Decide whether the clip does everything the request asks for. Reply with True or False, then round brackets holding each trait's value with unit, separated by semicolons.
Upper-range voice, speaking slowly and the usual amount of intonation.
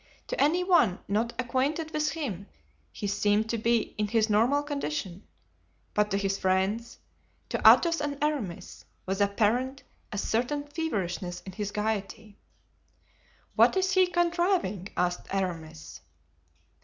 False (220 Hz; 125 wpm; 7.0 semitones)